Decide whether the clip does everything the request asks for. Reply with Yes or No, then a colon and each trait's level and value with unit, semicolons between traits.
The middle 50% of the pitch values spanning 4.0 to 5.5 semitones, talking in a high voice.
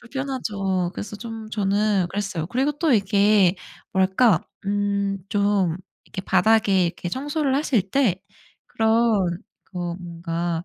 No: average, 3.4 semitones; high, 200 Hz